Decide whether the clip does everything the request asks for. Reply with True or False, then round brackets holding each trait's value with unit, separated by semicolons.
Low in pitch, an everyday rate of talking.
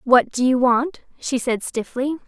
False (255 Hz; 185 wpm)